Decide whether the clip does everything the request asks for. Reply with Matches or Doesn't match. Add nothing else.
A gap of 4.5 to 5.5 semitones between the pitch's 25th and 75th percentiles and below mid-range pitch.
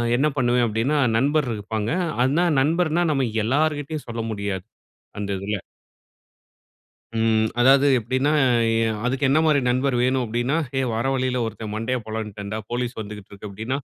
Doesn't match